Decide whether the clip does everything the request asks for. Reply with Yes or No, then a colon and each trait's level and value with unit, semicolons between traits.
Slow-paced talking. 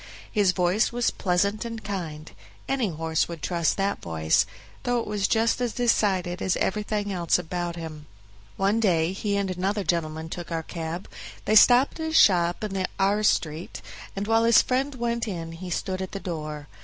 No: average, 180 wpm